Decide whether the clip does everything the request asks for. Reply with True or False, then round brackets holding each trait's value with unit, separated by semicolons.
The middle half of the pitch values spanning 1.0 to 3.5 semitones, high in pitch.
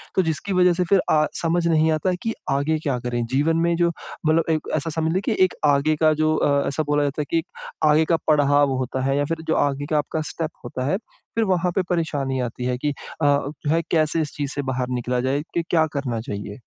False (2.7 semitones; 150 Hz)